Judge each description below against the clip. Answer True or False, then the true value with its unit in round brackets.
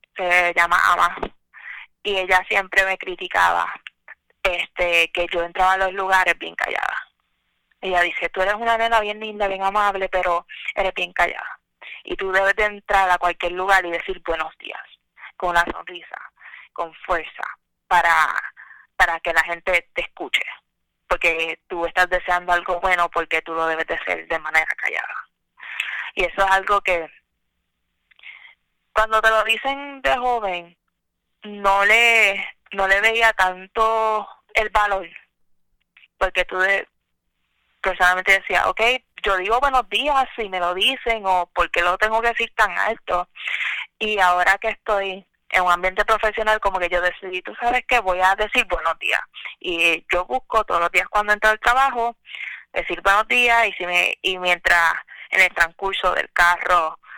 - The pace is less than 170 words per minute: True (160 wpm)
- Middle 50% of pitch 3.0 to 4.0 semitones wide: True (3.6 semitones)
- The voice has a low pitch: False (190 Hz)